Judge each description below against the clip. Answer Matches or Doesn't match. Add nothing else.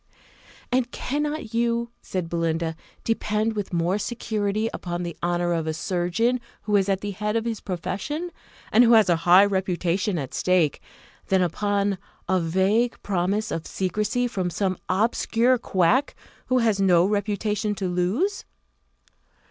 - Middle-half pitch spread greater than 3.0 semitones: Matches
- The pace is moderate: Matches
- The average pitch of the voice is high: Matches